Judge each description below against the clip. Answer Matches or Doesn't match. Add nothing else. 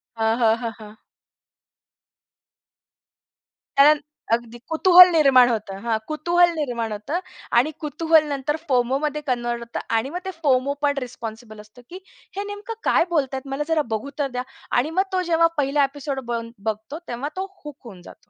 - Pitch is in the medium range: Doesn't match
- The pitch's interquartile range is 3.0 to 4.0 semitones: Doesn't match